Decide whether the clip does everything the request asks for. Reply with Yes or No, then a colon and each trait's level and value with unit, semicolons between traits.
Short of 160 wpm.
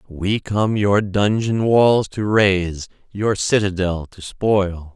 Yes: slow, 135 wpm